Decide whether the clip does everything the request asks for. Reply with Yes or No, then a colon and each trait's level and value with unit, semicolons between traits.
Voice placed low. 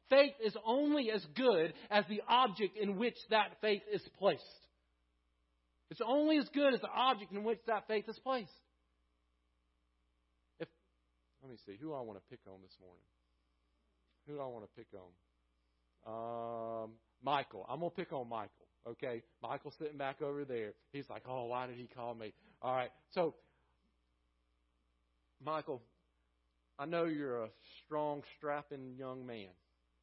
Yes: low, 120 Hz